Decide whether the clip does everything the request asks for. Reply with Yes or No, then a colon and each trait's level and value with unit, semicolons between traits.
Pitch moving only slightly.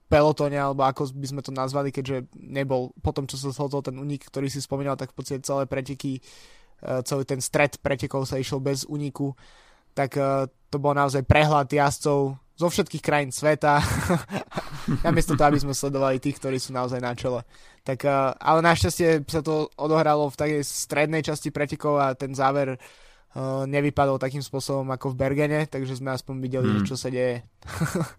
Yes: narrow, 1.7 semitones